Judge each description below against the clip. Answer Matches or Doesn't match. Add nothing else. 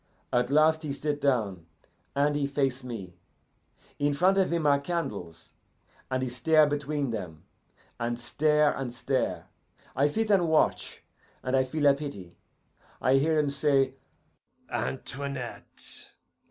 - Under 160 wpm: Matches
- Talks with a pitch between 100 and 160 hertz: Matches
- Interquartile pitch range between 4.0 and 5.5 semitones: Doesn't match